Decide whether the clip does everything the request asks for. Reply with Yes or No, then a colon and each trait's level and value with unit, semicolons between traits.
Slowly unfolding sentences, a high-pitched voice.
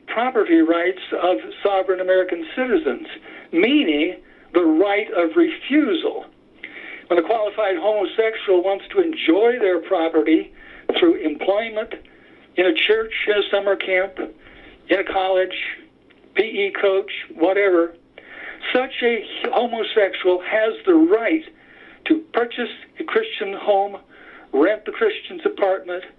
Yes: slow, 115 wpm; very high, 310 Hz